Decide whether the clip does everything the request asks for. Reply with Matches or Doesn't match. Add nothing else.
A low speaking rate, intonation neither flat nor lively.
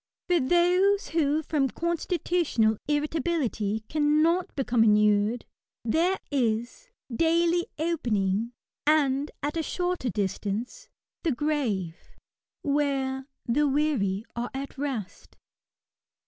Doesn't match